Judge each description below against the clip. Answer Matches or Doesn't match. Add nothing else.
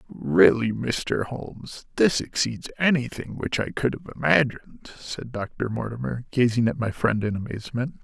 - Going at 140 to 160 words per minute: Matches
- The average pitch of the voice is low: Matches